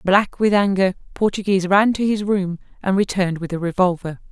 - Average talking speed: Yes, average, 180 wpm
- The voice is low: No, high, 190 Hz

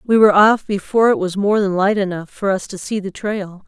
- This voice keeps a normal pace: No, fast, 260 wpm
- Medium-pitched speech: No, high, 200 Hz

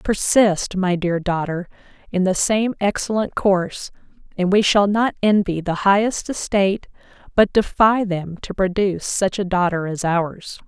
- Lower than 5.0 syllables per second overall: Yes, 4.4 syllables/s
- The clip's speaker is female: Yes, female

